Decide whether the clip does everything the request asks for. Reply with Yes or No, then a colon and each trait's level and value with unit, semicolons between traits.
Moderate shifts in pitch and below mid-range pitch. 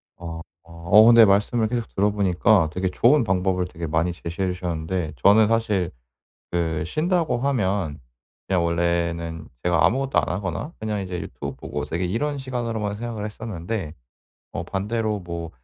Yes: average, 4.8 semitones; very low, 95 Hz